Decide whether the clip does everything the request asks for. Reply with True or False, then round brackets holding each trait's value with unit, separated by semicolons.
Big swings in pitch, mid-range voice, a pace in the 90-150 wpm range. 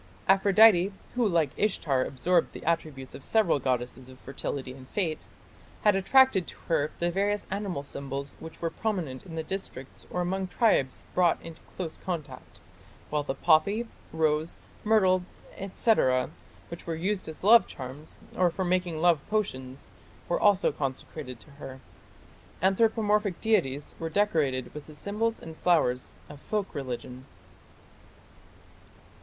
True (5.8 semitones; 165 Hz; 140 wpm)